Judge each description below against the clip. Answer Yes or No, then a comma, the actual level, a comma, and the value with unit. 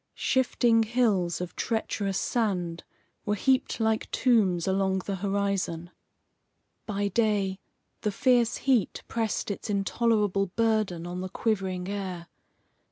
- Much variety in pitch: No, average, 3.1 semitones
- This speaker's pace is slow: Yes, slow, 115 wpm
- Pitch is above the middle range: Yes, high, 200 Hz